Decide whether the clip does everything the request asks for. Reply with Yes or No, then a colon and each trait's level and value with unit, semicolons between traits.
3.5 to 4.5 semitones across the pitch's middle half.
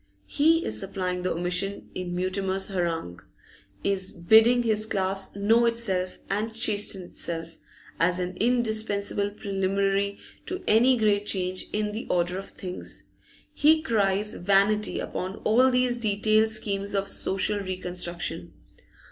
No: average, 2.9 semitones